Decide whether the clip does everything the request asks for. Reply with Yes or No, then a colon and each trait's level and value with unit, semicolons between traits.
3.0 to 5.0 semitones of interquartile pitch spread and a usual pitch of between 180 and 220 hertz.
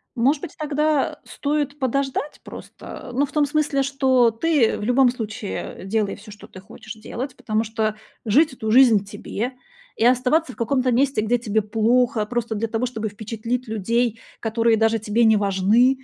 No: average, 3.6 semitones; high, 235 Hz